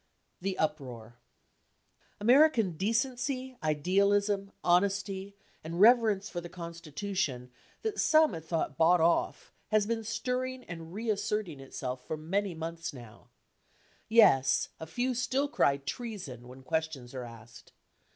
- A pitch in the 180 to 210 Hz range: Yes, medium, 185 Hz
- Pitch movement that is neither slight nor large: No, wide, 6.3 semitones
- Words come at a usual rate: No, slow, 130 wpm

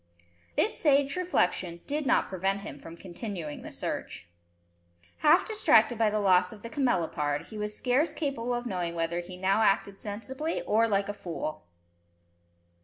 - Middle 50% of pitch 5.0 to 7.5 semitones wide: Yes, wide, 5.6 semitones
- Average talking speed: Yes, average, 160 wpm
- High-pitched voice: Yes, high, 205 Hz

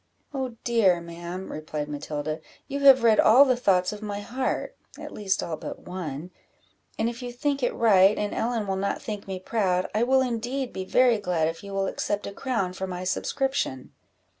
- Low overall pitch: No, high, 205 Hz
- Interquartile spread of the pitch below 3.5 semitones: No, average, 5.0 semitones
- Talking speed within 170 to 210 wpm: Yes, average, 195 wpm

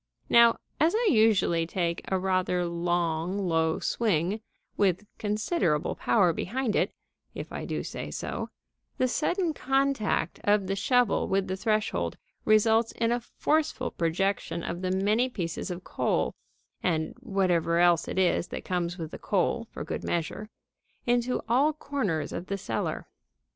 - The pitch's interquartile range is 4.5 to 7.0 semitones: Yes, average, 5.2 semitones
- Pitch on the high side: Yes, high, 195 Hz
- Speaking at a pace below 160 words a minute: Yes, average, 150 wpm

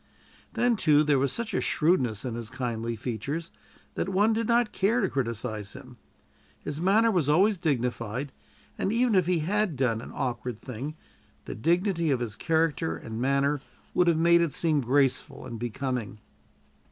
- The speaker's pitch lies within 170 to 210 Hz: No, medium, 145 Hz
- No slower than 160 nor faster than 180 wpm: Yes, average, 165 wpm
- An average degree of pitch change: No, wide, 6.4 semitones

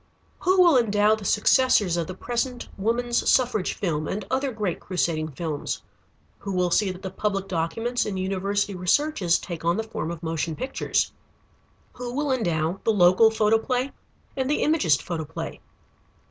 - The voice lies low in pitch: No, high, 200 Hz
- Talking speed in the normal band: Yes, average, 160 wpm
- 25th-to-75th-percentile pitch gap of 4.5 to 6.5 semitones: Yes, wide, 5.6 semitones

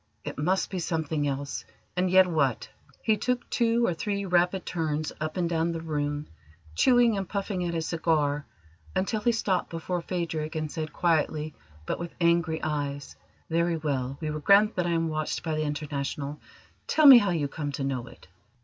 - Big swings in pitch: No, average, 3.5 semitones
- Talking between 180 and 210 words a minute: Yes, average, 185 wpm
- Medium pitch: Yes, medium, 165 Hz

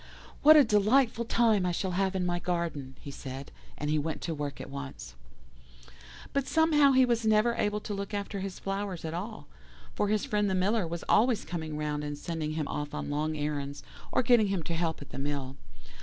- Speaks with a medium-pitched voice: Yes, medium, 180 Hz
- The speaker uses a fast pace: Yes, fast, 210 wpm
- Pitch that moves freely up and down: Yes, wide, 6.1 semitones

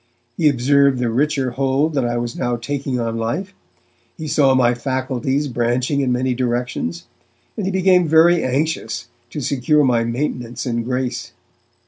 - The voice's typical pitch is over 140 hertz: No, low, 130 Hz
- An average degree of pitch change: Yes, average, 3.2 semitones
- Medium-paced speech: Yes, average, 155 wpm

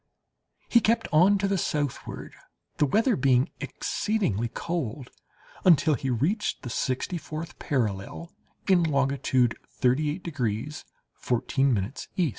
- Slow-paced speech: Yes, slow, 115 wpm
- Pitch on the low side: No, medium, 145 Hz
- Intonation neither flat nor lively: No, wide, 5.7 semitones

